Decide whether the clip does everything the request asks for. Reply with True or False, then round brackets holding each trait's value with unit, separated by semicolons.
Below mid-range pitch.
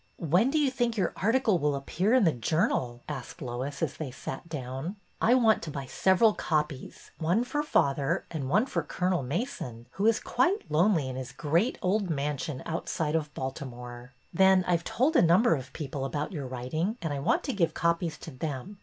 False (160 Hz)